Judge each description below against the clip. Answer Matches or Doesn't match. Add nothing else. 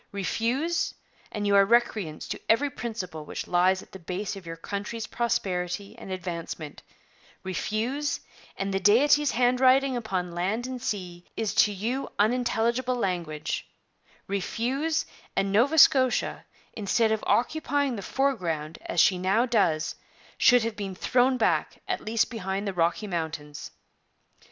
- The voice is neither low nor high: Doesn't match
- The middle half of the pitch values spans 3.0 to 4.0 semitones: Doesn't match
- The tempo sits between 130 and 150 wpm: Matches